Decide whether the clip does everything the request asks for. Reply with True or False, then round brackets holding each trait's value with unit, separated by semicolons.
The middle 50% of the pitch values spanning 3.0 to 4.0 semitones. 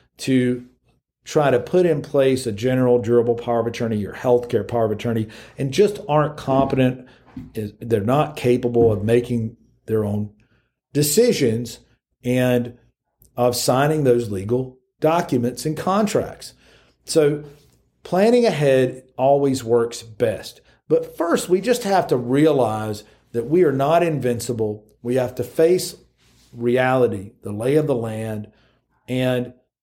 True (3.5 semitones)